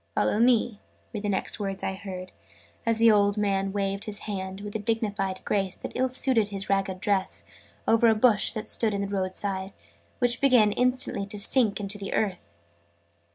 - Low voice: No, high, 205 Hz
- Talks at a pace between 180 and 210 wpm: Yes, average, 190 wpm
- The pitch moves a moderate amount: No, narrow, 2.3 semitones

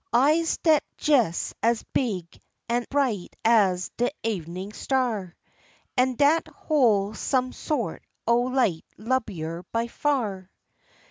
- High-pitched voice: Yes, high, 235 Hz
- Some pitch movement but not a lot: Yes, average, 5.0 semitones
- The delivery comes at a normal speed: No, slow, 115 wpm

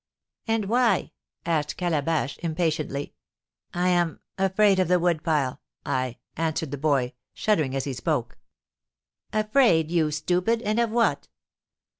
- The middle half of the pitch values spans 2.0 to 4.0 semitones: No, average, 4.5 semitones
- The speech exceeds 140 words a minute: No, slow, 135 wpm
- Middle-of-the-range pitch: Yes, medium, 165 Hz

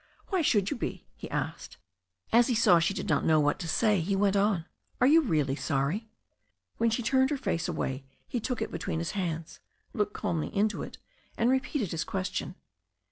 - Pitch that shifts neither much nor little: No, wide, 6.0 semitones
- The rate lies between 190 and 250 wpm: Yes, average, 195 wpm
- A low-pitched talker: No, high, 200 Hz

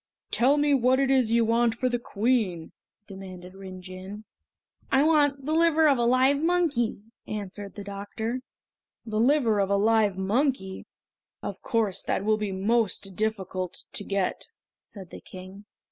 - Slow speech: No, average, 160 wpm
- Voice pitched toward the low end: No, high, 220 Hz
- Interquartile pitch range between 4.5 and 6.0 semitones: Yes, average, 4.9 semitones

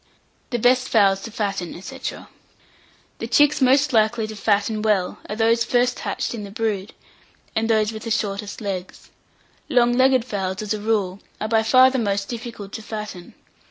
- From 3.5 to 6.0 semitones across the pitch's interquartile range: No, average, 2.9 semitones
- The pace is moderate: Yes, average, 175 wpm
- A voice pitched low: No, high, 220 Hz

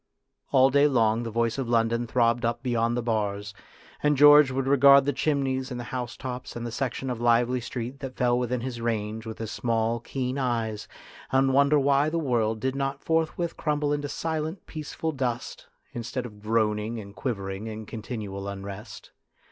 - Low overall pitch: Yes, low, 120 Hz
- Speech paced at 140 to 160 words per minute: No, average, 180 wpm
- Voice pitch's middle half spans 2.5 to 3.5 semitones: Yes, average, 3.2 semitones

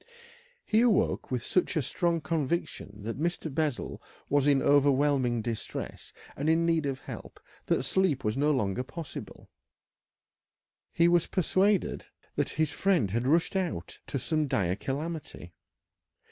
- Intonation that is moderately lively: Yes, average, 4.9 semitones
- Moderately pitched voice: Yes, medium, 145 Hz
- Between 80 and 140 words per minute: Yes, slow, 135 wpm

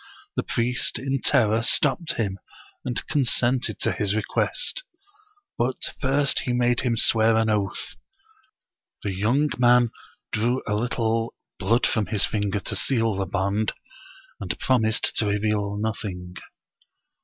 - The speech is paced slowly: Yes, slow, 130 wpm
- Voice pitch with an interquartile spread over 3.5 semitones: No, average, 2.9 semitones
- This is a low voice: Yes, low, 110 Hz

